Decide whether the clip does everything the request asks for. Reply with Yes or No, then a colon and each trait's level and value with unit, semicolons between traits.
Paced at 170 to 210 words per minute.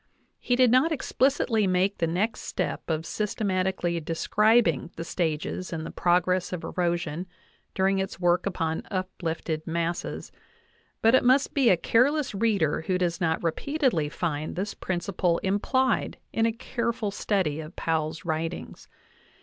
No: average, 140 wpm